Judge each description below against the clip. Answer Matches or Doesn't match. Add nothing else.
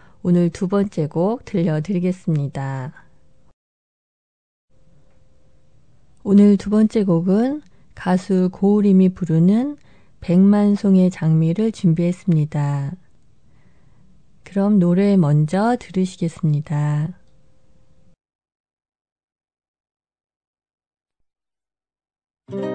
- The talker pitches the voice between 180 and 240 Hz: Matches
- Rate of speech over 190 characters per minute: Doesn't match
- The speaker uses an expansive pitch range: Doesn't match